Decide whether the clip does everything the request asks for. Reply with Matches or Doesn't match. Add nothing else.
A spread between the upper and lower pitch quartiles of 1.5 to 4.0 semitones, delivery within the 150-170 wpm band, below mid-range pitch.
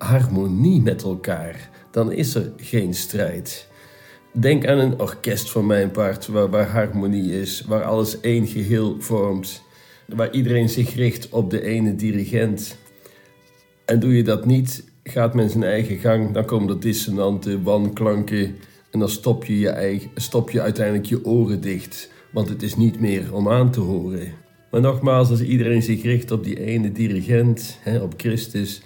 Matches